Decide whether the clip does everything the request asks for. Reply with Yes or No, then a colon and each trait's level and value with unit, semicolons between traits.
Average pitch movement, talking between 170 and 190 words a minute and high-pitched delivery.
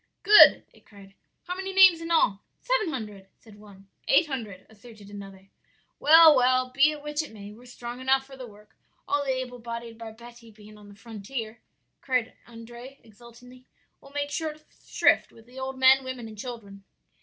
Yes: average, 4.0 semitones; average, 180 wpm; high, 240 Hz